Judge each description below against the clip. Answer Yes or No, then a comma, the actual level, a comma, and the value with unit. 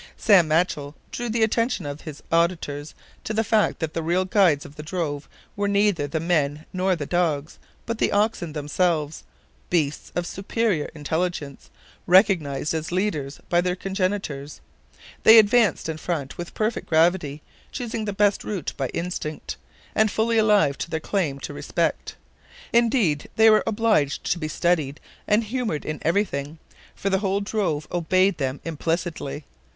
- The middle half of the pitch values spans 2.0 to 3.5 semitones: No, average, 5.2 semitones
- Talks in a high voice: No, medium, 175 Hz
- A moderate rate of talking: Yes, average, 155 wpm